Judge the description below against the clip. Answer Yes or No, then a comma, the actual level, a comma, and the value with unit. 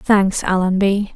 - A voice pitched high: Yes, high, 195 Hz